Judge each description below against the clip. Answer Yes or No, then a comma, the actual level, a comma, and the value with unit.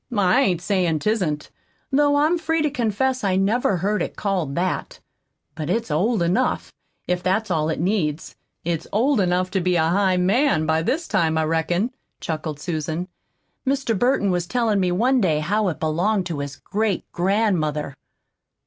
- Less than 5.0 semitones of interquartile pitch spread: No, average, 5.3 semitones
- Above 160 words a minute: Yes, average, 170 wpm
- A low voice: No, medium, 185 Hz